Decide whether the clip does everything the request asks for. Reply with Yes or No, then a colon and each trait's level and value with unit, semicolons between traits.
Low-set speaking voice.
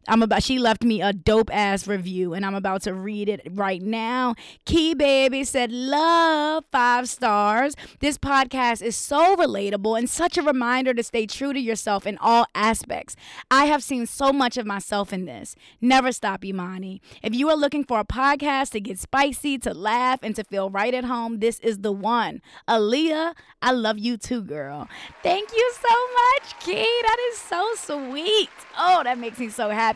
No: high, 245 Hz